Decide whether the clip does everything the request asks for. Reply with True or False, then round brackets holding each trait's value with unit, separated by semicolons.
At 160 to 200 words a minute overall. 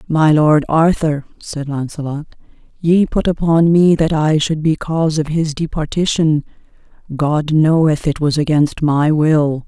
False (150 wpm)